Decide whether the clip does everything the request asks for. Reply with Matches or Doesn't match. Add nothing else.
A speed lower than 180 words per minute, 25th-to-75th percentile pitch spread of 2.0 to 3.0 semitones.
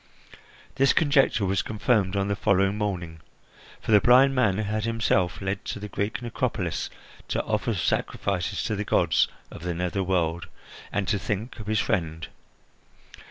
Matches